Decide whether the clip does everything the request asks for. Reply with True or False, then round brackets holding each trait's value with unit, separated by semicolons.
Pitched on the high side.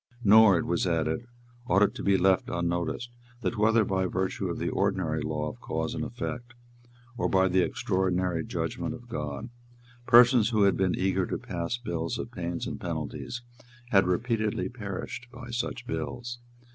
False (95 Hz)